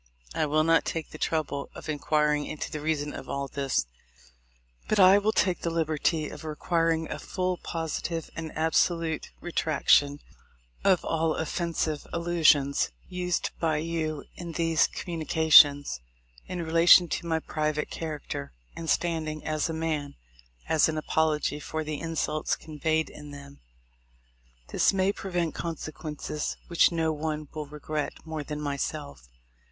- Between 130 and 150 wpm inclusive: Yes, average, 145 wpm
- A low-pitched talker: No, medium, 160 Hz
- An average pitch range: No, narrow, 1.7 semitones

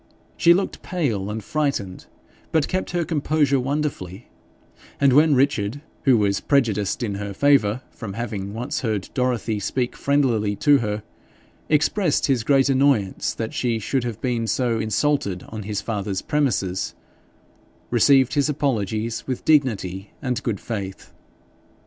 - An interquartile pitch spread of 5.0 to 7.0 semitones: Yes, average, 5.3 semitones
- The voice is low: Yes, low, 120 Hz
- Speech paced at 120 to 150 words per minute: Yes, average, 140 wpm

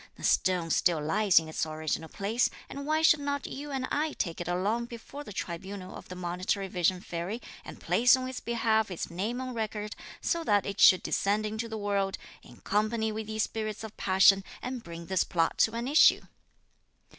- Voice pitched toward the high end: Yes, high, 210 Hz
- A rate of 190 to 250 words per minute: Yes, average, 200 wpm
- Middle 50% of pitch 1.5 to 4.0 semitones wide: No, average, 4.4 semitones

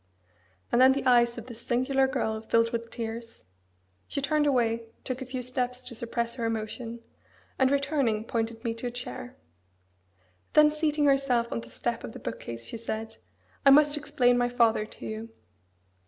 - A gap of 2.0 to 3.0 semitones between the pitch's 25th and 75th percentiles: Yes, average, 2.7 semitones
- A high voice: Yes, high, 240 Hz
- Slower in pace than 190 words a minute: Yes, average, 180 wpm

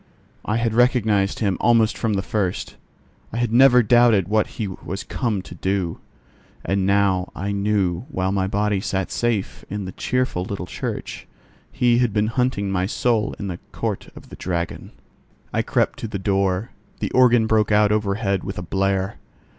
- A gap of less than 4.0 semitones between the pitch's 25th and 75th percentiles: Yes, average, 2.9 semitones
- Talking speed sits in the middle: Yes, average, 175 wpm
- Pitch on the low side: Yes, low, 100 Hz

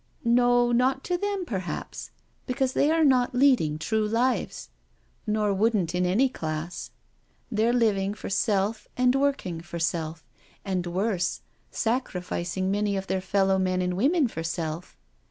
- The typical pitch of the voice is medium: No, high, 205 Hz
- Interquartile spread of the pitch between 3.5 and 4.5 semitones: No, wide, 5.5 semitones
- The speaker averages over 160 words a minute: No, average, 155 wpm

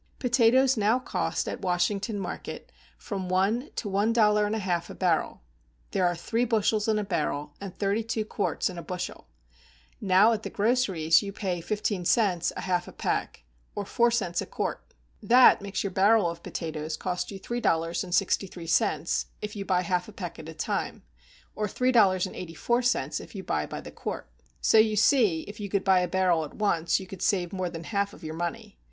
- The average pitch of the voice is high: Yes, high, 195 Hz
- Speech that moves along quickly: Yes, fast, 215 wpm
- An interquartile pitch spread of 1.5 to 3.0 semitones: No, average, 3.5 semitones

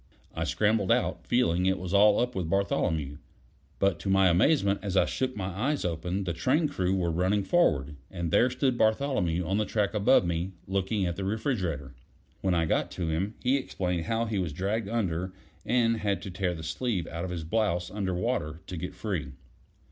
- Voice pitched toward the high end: No, very low, 95 Hz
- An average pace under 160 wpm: No, average, 200 wpm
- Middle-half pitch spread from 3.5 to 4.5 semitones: Yes, average, 4.2 semitones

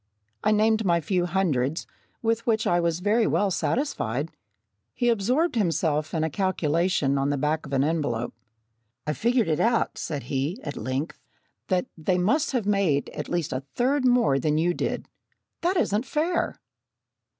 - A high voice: No, medium, 175 Hz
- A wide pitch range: Yes, wide, 6.9 semitones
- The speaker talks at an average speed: Yes, average, 160 wpm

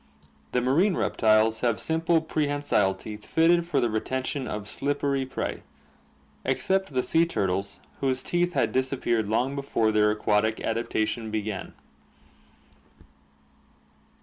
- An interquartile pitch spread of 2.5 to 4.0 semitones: No, average, 5.0 semitones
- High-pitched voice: No, low, 125 Hz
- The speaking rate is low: Yes, slow, 120 wpm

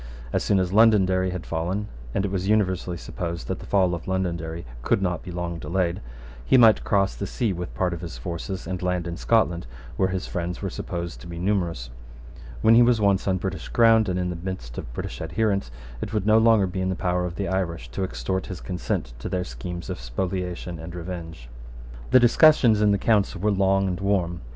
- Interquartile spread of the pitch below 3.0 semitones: Yes, narrow, 2.5 semitones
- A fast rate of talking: Yes, fast, 215 wpm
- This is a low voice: Yes, very low, 90 Hz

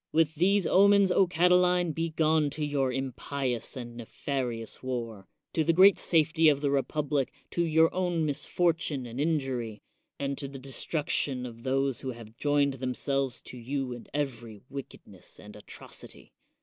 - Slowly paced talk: No, average, 155 wpm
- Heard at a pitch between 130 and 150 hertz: Yes, medium, 140 Hz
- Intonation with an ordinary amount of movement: Yes, average, 4.0 semitones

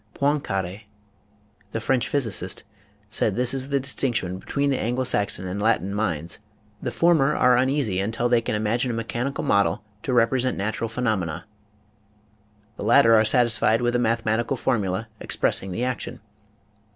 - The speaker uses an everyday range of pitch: Yes, average, 3.7 semitones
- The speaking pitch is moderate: No, low, 115 Hz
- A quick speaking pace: No, average, 155 wpm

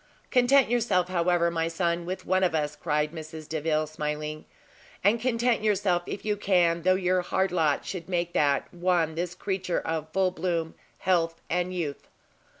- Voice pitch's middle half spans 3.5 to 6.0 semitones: No, narrow, 2.6 semitones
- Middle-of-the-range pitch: Yes, medium, 175 Hz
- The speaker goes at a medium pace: Yes, average, 165 wpm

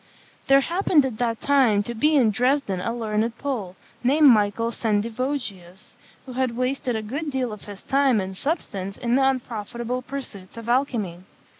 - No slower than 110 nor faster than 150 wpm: No, average, 165 wpm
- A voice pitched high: Yes, high, 240 Hz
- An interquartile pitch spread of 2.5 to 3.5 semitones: No, average, 4.1 semitones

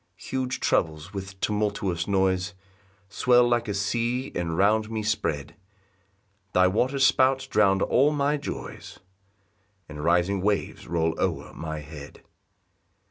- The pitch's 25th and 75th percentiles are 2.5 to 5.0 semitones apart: No, wide, 5.6 semitones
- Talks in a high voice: No, low, 100 Hz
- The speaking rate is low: Yes, slow, 130 wpm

